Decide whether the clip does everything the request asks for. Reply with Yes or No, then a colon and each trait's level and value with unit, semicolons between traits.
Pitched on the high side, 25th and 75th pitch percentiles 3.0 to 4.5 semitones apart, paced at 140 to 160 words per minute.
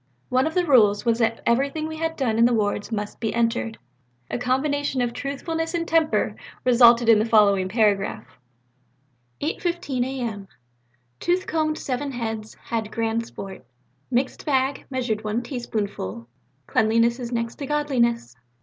Yes: high, 235 Hz; average, 4.0 semitones; average, 150 wpm